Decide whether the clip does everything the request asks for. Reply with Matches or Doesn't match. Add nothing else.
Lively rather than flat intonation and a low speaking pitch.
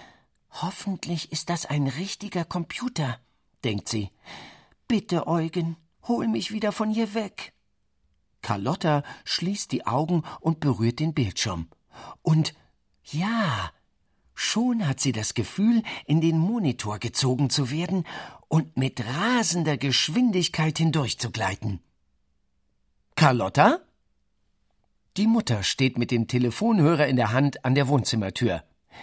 Doesn't match